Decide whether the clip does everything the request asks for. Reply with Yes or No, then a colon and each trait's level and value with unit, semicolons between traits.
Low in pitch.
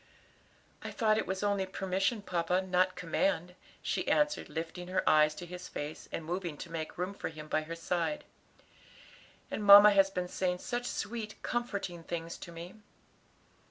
No: medium, 180 Hz